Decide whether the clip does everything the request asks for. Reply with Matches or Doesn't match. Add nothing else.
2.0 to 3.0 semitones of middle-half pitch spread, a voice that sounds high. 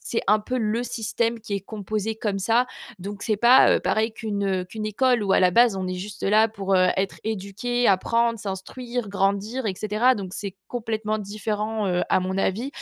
Matches